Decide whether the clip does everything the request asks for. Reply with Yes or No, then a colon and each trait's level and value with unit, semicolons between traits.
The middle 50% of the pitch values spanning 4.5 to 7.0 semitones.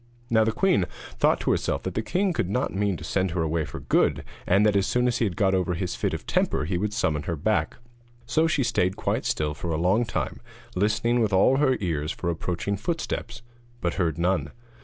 Yes: average, 4.8 semitones